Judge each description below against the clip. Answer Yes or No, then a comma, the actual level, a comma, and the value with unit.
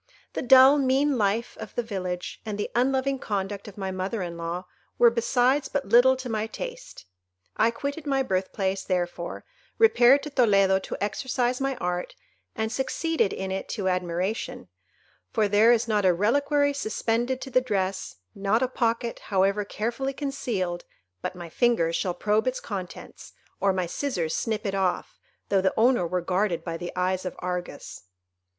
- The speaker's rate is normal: Yes, average, 170 wpm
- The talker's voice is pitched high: Yes, high, 215 Hz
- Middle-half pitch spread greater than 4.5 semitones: Yes, average, 5.3 semitones